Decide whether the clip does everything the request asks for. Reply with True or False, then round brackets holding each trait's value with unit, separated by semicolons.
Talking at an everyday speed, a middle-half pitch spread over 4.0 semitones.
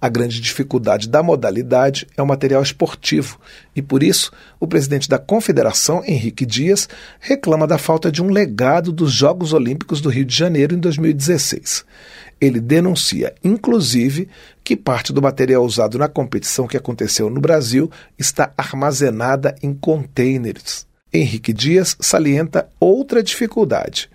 True (140 wpm; 4.6 semitones)